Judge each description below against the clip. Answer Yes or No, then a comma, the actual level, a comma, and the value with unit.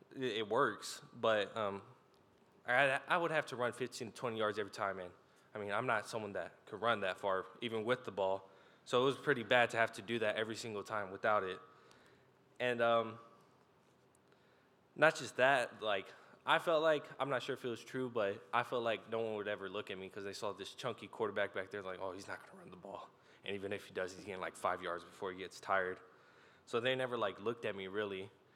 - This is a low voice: Yes, low, 115 Hz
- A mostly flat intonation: No, average, 3.9 semitones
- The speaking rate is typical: No, fast, 235 wpm